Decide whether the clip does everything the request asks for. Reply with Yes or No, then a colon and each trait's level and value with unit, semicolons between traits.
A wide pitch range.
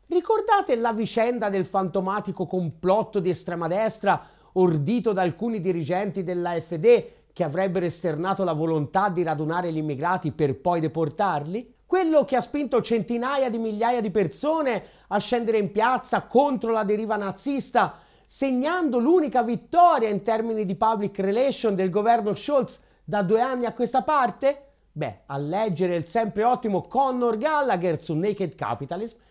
No: average, 5.0 semitones